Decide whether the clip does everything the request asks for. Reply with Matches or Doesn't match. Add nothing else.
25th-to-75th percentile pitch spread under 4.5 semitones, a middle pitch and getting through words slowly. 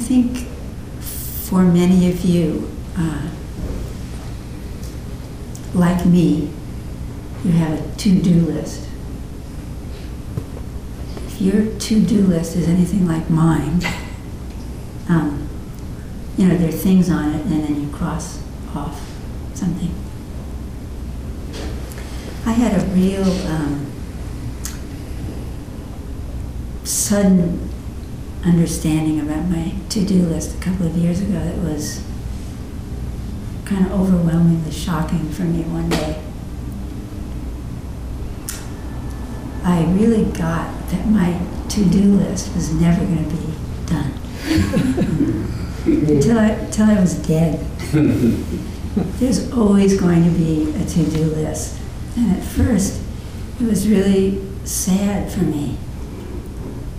Matches